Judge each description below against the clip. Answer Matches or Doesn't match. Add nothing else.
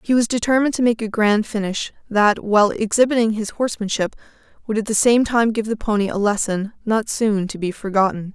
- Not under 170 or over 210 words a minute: Matches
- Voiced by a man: Doesn't match